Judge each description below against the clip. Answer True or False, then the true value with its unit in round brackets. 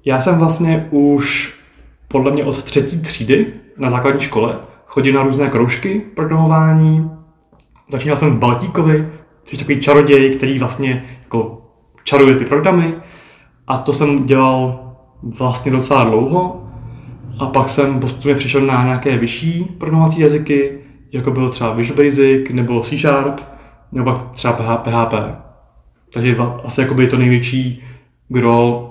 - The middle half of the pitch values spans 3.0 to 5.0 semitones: False (2.6 semitones)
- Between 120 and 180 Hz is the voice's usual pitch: True (135 Hz)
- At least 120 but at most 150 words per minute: True (135 wpm)